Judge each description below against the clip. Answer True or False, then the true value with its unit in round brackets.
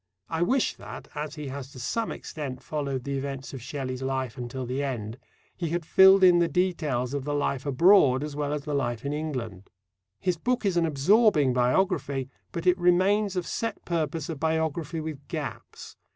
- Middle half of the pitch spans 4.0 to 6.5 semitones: True (4.5 semitones)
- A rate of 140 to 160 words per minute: False (190 wpm)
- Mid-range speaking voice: True (150 Hz)